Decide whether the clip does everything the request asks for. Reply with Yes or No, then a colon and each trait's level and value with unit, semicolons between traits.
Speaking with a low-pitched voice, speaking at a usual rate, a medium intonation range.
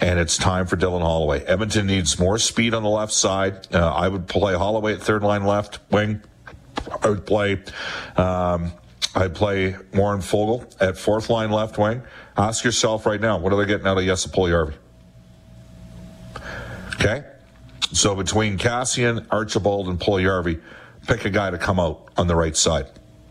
Yes: very low, 95 Hz; average, 175 wpm; average, 3.1 semitones